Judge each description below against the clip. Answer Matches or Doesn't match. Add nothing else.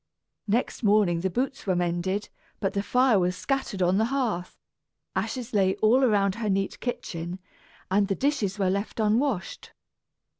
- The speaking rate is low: Doesn't match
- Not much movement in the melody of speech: Doesn't match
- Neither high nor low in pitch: Doesn't match